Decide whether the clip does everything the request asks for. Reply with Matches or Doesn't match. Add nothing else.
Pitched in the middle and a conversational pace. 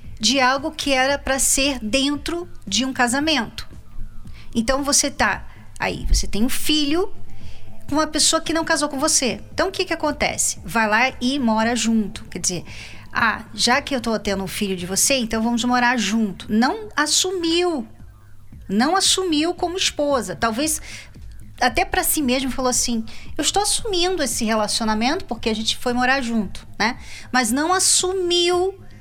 Doesn't match